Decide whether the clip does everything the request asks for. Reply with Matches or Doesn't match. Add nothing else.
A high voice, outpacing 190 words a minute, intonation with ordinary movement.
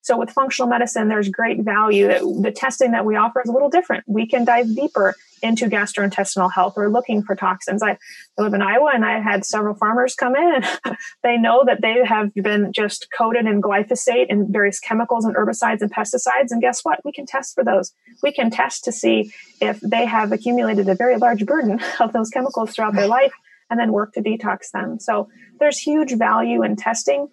Matches